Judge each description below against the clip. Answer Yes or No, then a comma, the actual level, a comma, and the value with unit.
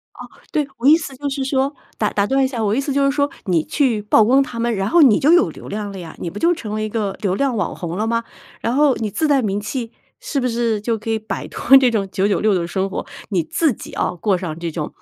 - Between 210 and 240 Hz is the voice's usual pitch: Yes, high, 225 Hz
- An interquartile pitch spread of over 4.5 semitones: Yes, average, 5.2 semitones